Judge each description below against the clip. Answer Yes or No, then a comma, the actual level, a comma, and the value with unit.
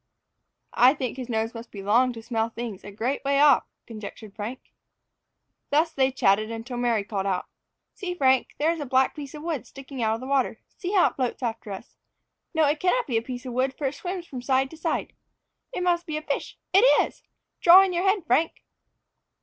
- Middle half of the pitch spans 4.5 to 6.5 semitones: Yes, average, 5.1 semitones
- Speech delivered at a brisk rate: Yes, fast, 215 wpm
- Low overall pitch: No, very high, 260 Hz